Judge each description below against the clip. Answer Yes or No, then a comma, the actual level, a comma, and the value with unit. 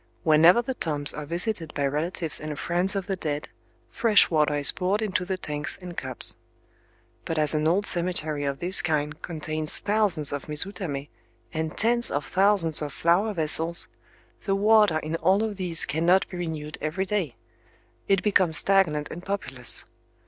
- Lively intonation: No, average, 4.2 semitones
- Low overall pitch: No, medium, 165 Hz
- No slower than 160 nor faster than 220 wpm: Yes, average, 165 wpm